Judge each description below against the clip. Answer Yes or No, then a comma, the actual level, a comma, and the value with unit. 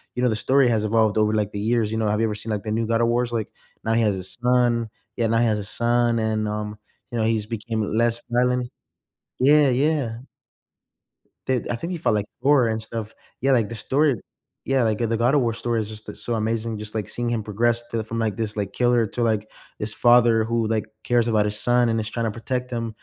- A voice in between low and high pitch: No, low, 115 Hz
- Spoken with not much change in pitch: Yes, narrow, 1.9 semitones